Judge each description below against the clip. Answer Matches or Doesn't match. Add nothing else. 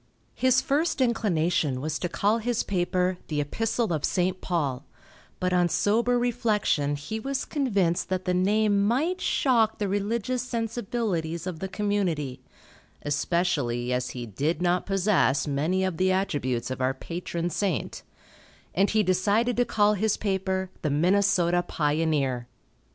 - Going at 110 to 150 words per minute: Matches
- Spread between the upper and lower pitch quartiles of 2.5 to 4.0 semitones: Doesn't match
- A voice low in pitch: Doesn't match